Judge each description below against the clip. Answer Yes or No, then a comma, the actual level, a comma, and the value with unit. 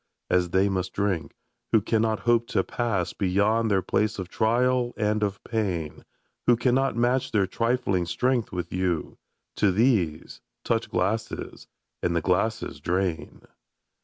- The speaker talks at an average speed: Yes, average, 145 wpm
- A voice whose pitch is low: Yes, low, 105 Hz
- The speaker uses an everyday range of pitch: Yes, average, 4.2 semitones